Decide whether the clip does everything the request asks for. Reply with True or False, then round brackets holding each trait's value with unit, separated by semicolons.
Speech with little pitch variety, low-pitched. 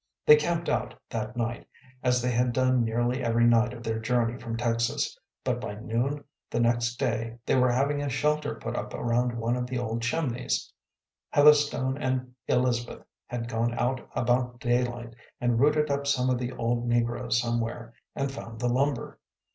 True (1.7 semitones; 120 Hz)